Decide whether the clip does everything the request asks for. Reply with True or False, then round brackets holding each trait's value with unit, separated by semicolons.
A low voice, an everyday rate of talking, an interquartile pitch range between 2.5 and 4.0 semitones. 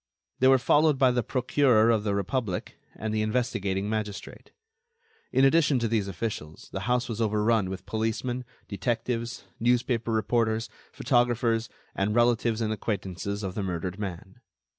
True (110 Hz; 145 wpm; 3.2 semitones)